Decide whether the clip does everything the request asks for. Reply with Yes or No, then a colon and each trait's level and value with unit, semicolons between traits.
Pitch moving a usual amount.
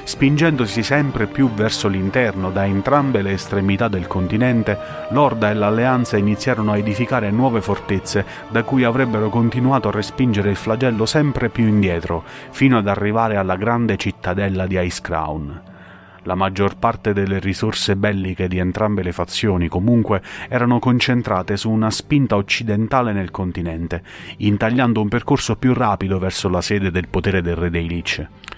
Yes: average, 4.0 semitones